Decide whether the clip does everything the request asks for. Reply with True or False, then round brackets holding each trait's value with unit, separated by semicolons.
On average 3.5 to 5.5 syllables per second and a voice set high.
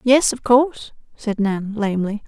True (4.7 syllables/s; 225 Hz)